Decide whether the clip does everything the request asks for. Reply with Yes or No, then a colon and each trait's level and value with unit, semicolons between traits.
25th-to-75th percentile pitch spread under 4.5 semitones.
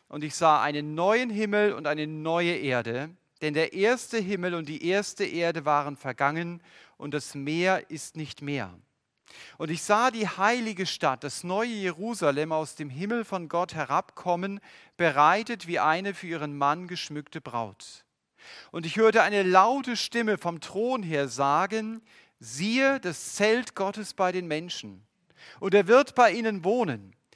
No: wide, 5.5 semitones